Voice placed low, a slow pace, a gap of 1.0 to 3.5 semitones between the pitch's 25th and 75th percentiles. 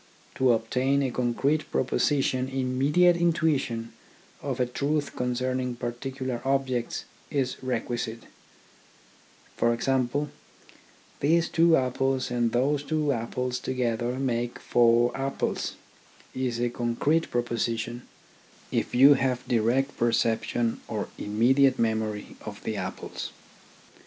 Yes: low, 125 Hz; slow, 110 wpm; narrow, 2.4 semitones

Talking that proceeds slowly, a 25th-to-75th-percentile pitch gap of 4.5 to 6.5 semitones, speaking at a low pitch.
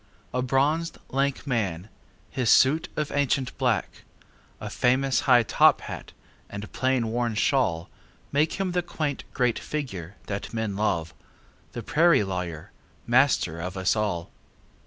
Yes: slow, 125 wpm; wide, 5.6 semitones; low, 125 Hz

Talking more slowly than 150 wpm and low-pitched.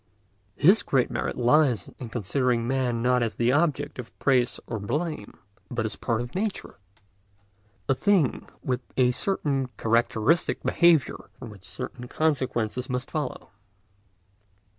Yes: average, 140 wpm; low, 125 Hz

